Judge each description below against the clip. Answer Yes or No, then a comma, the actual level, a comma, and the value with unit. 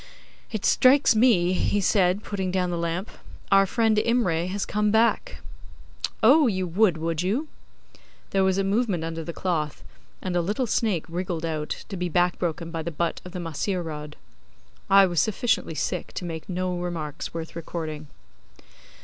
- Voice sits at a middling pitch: Yes, medium, 180 Hz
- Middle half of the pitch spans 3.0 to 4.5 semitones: Yes, average, 3.6 semitones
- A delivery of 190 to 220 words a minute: No, average, 170 wpm